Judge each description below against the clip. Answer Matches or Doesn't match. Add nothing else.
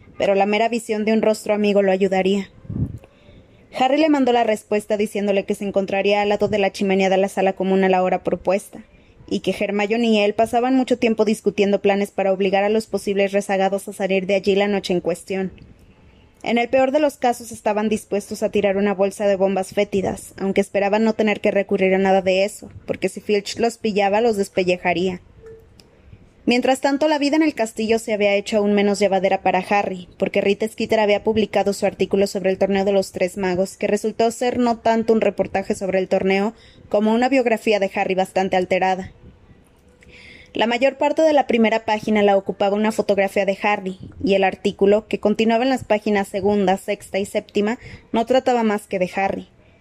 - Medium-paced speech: Doesn't match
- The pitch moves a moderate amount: Doesn't match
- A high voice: Matches